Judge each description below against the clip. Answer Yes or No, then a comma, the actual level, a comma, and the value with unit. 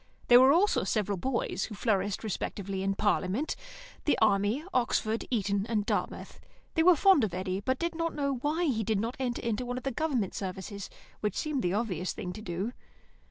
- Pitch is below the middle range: No, high, 220 Hz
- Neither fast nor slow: Yes, average, 190 wpm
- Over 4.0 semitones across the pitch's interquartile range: Yes, average, 5.0 semitones